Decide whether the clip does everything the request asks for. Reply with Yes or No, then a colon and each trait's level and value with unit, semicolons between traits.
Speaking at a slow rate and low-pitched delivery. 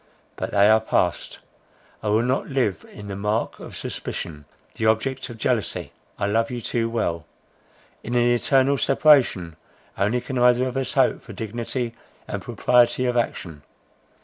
No: average, 155 wpm; low, 115 Hz